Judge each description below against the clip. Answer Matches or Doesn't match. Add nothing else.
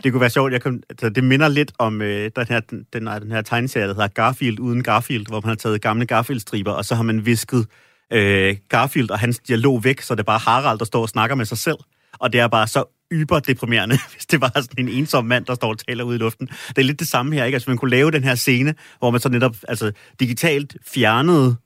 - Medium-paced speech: Doesn't match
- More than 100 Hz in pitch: Matches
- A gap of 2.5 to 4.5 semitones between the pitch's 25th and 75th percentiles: Matches